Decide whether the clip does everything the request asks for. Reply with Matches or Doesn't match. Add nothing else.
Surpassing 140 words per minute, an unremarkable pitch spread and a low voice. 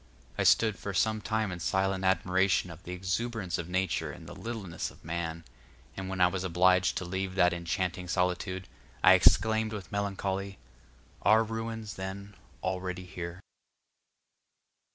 Doesn't match